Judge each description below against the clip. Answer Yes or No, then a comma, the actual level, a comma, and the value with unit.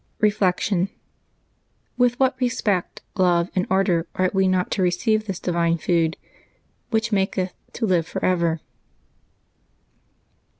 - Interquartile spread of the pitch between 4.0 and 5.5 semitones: No, average, 3.4 semitones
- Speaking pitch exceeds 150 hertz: Yes, medium, 185 Hz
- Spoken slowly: Yes, slow, 120 wpm